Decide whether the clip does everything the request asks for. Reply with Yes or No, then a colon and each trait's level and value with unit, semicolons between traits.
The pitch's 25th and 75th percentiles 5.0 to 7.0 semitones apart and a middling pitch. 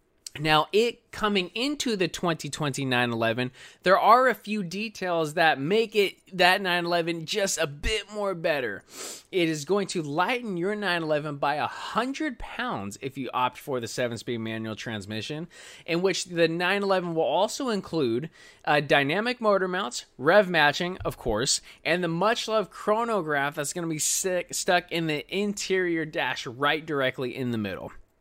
Yes: wide, 5.6 semitones; medium, 175 Hz